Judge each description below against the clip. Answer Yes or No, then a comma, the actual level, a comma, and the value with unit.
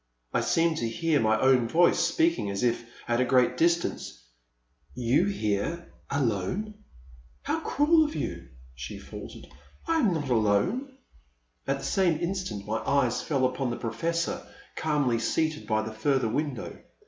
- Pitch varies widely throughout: Yes, wide, 6.9 semitones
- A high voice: No, low, 135 Hz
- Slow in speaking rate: No, average, 160 wpm